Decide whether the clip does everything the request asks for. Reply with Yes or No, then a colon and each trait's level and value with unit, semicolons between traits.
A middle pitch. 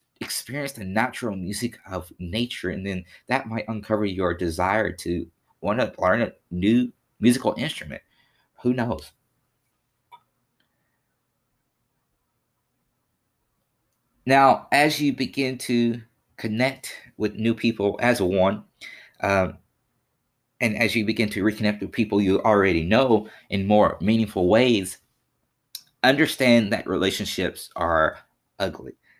No: low, 115 Hz